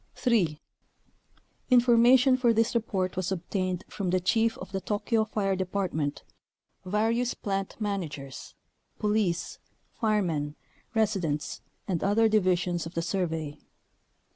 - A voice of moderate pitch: No, high, 195 Hz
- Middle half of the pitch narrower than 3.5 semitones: No, average, 4.1 semitones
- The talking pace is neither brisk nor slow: No, slow, 115 wpm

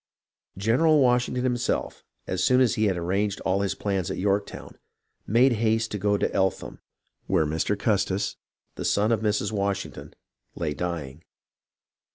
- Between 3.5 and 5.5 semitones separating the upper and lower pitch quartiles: No, average, 3.0 semitones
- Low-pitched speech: Yes, low, 100 Hz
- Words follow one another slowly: No, average, 150 wpm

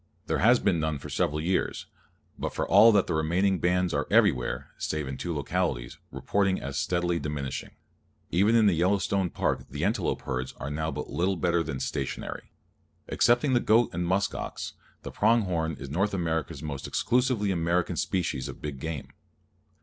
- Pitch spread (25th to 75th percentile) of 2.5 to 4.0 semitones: No, average, 4.4 semitones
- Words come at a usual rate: Yes, average, 175 wpm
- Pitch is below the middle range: Yes, very low, 85 Hz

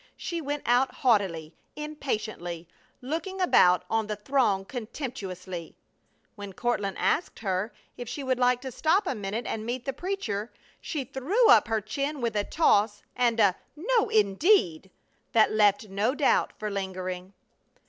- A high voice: Yes, high, 225 Hz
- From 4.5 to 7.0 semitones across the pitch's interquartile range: Yes, wide, 5.6 semitones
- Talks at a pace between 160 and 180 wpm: No, average, 150 wpm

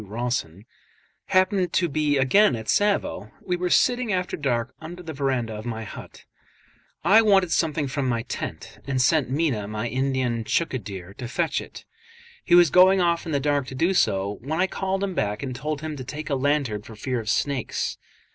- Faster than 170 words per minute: Yes, average, 195 wpm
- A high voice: No, medium, 140 Hz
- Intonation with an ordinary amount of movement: No, wide, 6.5 semitones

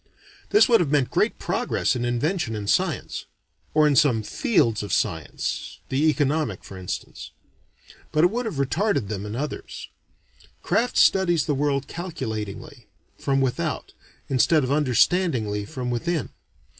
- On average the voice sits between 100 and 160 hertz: Yes, medium, 140 Hz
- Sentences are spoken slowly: No, average, 145 wpm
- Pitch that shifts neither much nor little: No, wide, 5.8 semitones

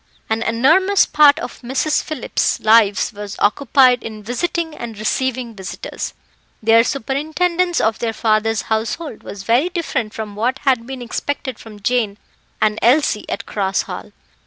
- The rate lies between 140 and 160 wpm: Yes, average, 150 wpm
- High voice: Yes, high, 235 Hz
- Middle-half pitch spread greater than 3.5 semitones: Yes, average, 4.5 semitones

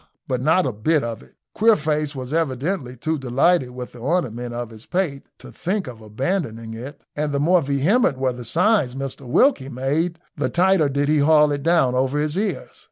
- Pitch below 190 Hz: Yes, medium, 140 Hz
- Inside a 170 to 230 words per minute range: Yes, average, 200 wpm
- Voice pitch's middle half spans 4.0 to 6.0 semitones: Yes, average, 4.7 semitones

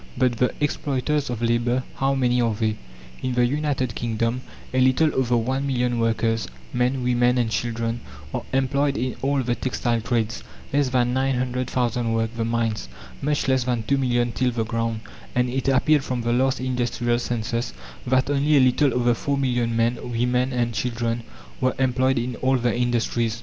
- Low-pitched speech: Yes, low, 125 Hz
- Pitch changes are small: Yes, narrow, 1.8 semitones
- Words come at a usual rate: Yes, average, 180 wpm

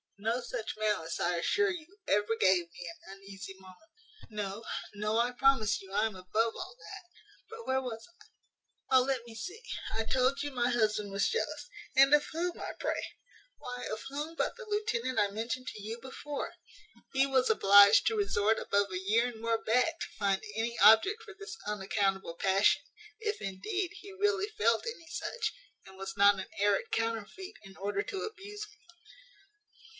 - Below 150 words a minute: No, average, 180 wpm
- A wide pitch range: Yes, wide, 7.6 semitones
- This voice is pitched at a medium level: No, high, 230 Hz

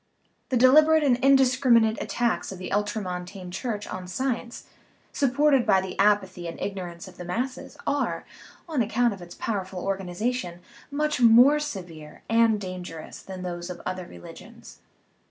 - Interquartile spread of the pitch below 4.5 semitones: No, wide, 5.6 semitones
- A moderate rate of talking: Yes, average, 145 wpm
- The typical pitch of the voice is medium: No, high, 205 Hz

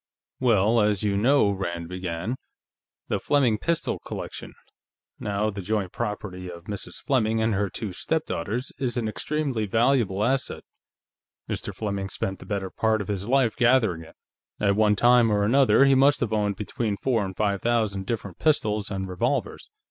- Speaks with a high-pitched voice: No, low, 105 Hz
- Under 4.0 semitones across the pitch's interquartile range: Yes, average, 3.4 semitones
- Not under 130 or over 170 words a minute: Yes, average, 165 wpm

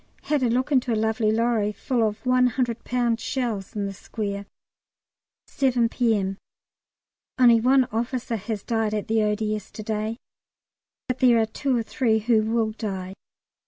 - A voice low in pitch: No, high, 225 Hz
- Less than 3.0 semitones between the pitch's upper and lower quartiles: Yes, narrow, 2.4 semitones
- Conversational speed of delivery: Yes, average, 160 wpm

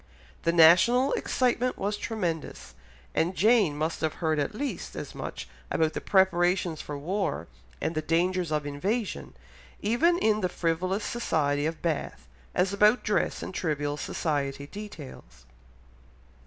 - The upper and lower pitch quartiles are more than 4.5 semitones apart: Yes, average, 5.3 semitones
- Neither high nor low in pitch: Yes, medium, 175 Hz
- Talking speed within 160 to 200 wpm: No, average, 140 wpm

